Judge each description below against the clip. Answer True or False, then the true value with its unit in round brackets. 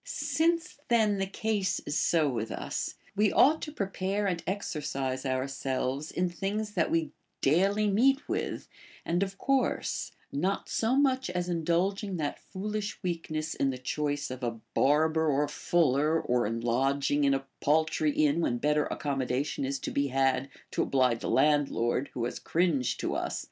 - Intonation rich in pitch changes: True (6.2 semitones)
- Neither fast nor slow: True (165 wpm)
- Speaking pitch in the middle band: True (155 Hz)